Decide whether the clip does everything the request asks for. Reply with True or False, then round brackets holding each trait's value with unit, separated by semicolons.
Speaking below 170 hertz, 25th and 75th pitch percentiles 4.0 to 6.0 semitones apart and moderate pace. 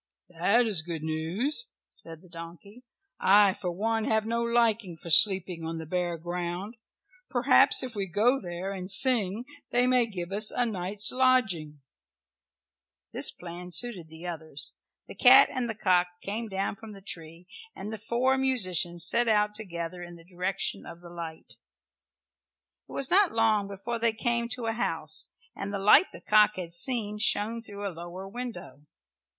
False (200 Hz; 4.9 semitones; 170 wpm)